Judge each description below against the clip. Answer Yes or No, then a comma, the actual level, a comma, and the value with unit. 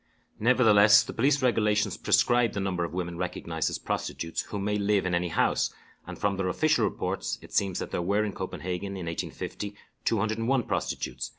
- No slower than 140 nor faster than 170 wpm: No, average, 180 wpm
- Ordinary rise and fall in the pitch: Yes, average, 3.3 semitones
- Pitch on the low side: Yes, low, 100 Hz